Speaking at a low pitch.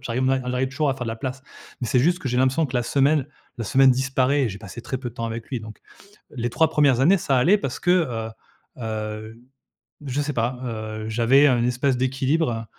Yes: low, 125 Hz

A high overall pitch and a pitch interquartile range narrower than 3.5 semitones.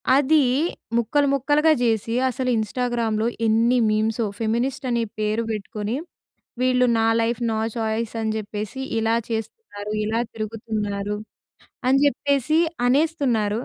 Yes: high, 230 Hz; average, 2.9 semitones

